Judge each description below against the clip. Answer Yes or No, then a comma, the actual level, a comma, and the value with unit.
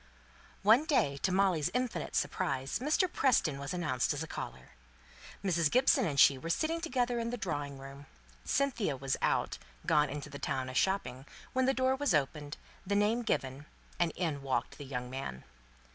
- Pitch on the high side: No, medium, 160 Hz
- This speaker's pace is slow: No, average, 175 wpm